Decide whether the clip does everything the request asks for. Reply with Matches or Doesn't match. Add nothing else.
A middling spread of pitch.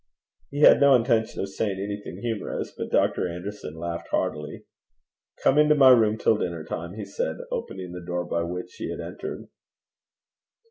Matches